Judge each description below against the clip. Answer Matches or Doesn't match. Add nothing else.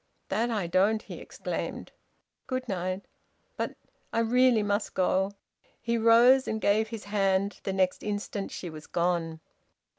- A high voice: Matches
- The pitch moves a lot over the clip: Doesn't match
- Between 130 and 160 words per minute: Matches